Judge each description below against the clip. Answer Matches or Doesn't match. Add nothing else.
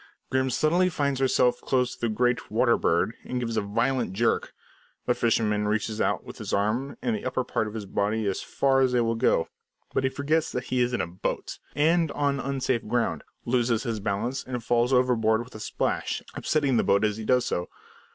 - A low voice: Matches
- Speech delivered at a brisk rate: Matches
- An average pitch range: Matches